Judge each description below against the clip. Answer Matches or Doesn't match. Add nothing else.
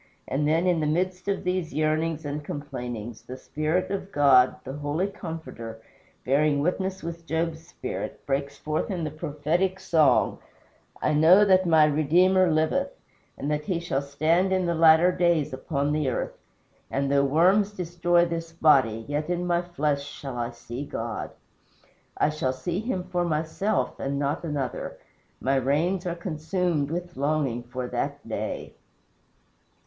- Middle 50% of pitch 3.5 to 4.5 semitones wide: Matches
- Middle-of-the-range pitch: Matches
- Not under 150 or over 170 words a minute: Matches